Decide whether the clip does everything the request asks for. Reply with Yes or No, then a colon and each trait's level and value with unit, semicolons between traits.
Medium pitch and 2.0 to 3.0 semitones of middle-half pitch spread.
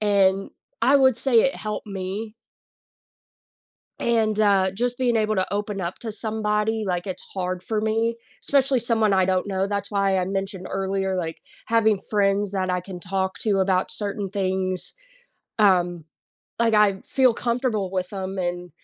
No: high, 200 Hz; narrow, 2.6 semitones